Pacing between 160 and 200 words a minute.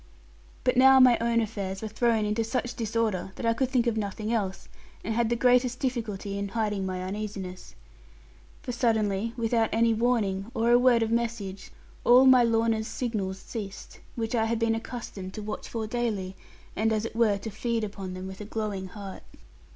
Yes: average, 190 wpm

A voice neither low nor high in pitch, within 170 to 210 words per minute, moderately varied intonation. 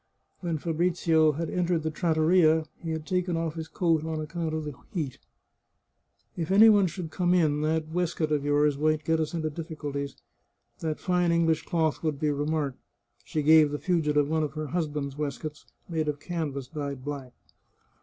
No: medium, 155 Hz; average, 180 wpm; narrow, 2.1 semitones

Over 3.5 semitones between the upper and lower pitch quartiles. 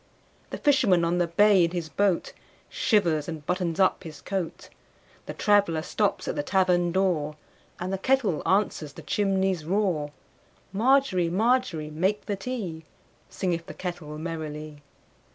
Yes: average, 3.9 semitones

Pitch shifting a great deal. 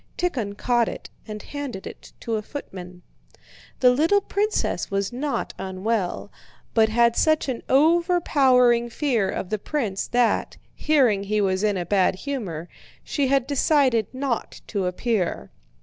Yes: wide, 5.9 semitones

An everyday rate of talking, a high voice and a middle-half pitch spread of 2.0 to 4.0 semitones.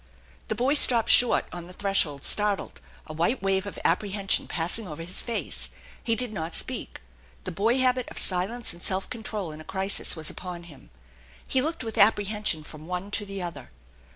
No: average, 185 wpm; high, 195 Hz; average, 4.5 semitones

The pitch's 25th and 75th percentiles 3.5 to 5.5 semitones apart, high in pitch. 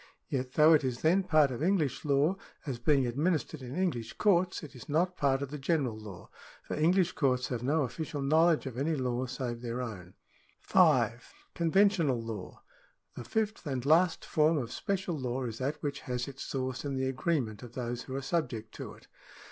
No: average, 4.4 semitones; medium, 140 Hz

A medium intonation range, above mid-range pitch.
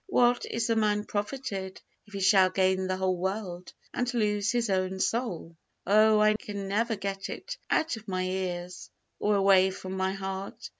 No: narrow, 2.2 semitones; high, 195 Hz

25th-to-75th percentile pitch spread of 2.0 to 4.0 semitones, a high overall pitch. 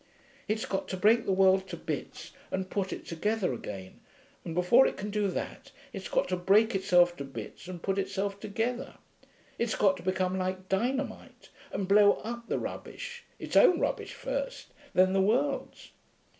Yes: average, 3.3 semitones; high, 195 Hz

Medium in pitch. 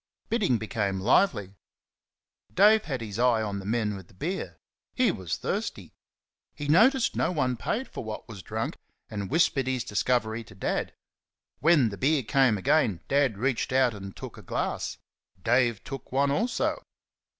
No: low, 125 Hz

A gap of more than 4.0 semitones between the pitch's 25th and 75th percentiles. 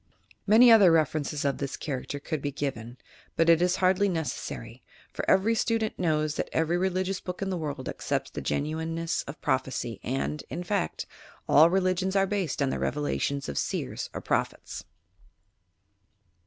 Yes: average, 4.7 semitones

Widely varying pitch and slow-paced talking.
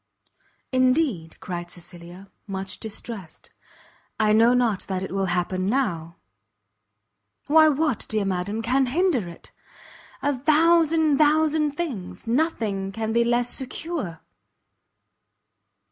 Yes: wide, 7.4 semitones; slow, 110 wpm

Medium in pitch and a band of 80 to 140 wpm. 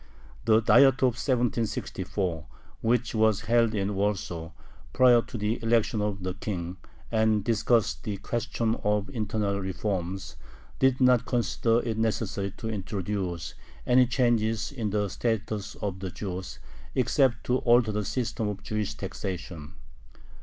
No: low, 110 Hz; slow, 135 wpm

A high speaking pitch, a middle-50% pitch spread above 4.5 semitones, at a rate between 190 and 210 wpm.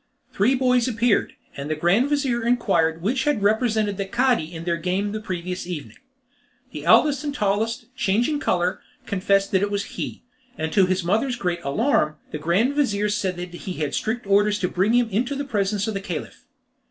Yes: high, 205 Hz; average, 4.9 semitones; average, 195 wpm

